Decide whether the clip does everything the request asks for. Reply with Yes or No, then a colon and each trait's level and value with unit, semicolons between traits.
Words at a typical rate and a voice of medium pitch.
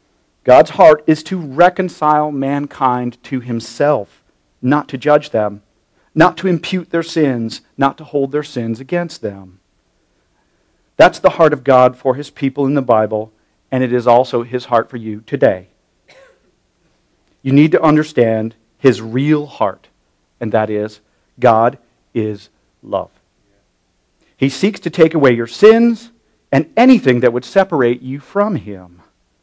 No: average, 145 wpm; low, 130 Hz